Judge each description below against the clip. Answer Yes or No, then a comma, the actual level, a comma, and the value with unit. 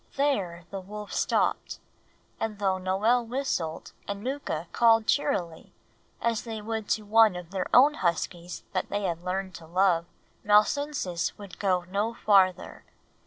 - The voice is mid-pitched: No, high, 200 Hz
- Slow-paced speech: No, average, 145 wpm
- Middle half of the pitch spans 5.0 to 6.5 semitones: No, average, 3.8 semitones